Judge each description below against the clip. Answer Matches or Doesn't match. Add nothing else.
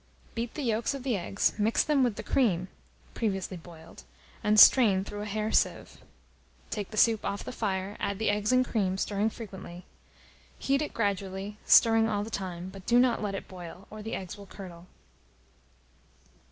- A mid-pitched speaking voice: Doesn't match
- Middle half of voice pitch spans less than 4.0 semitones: Matches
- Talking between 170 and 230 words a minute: Matches